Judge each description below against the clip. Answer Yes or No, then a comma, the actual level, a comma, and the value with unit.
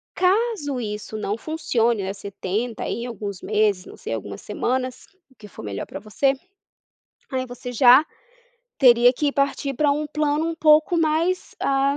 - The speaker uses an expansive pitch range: Yes, wide, 6.0 semitones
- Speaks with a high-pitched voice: Yes, very high, 255 Hz